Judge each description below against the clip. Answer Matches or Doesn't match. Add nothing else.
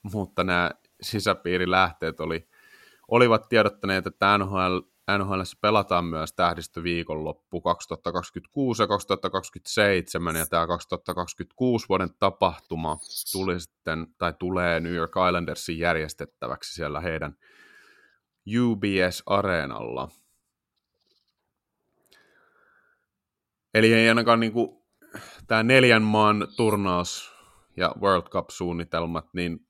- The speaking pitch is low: Matches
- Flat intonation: Doesn't match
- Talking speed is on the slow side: Matches